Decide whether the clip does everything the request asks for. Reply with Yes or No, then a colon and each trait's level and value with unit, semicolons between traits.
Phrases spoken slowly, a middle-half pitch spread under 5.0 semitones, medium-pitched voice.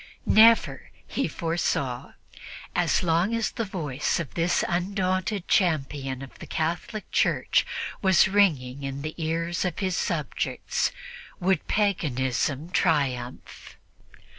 No: slow, 115 wpm; average, 5.3 semitones; medium, 165 Hz